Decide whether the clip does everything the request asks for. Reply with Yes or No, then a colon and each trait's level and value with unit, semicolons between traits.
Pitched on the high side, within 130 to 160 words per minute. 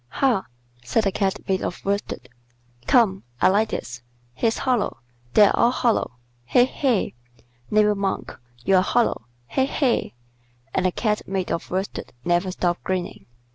Yes: high, 195 Hz; average, 145 wpm